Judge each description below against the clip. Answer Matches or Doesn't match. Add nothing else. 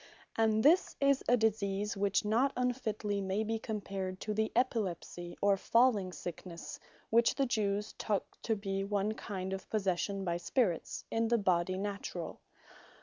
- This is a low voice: Doesn't match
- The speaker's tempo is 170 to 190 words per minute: Doesn't match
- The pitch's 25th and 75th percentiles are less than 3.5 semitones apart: Matches